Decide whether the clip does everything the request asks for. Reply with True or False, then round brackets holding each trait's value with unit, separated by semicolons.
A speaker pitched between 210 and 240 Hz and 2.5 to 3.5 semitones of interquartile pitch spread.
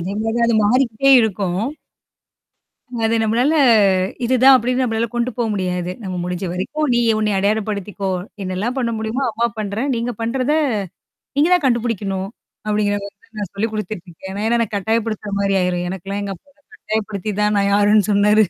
True (215 Hz; 2.9 semitones)